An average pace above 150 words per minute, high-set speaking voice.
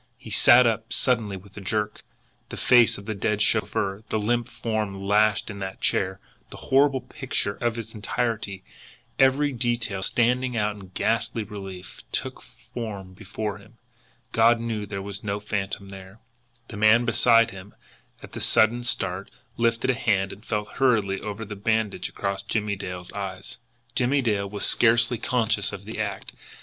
No: average, 165 wpm; low, 105 Hz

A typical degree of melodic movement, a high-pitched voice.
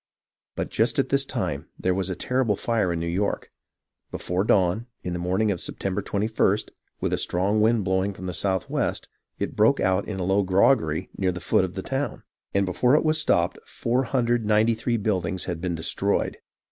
No: average, 3.3 semitones; very low, 95 Hz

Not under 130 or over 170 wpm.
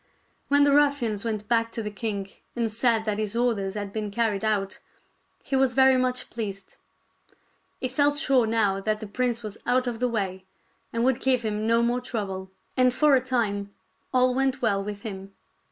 No: average, 190 wpm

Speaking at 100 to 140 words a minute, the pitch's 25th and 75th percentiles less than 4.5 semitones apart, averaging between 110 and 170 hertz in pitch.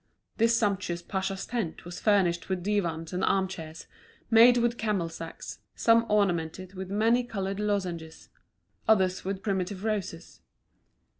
No: slow, 135 wpm; average, 3.3 semitones; high, 195 Hz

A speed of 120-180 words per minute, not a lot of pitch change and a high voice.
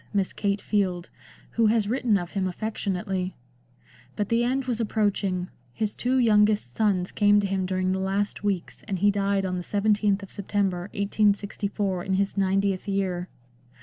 Yes: average, 165 wpm; narrow, 1.8 semitones; high, 200 Hz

